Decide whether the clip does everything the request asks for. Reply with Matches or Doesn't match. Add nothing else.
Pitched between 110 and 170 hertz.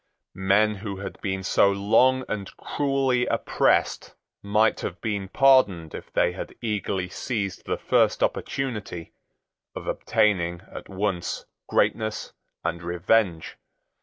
Doesn't match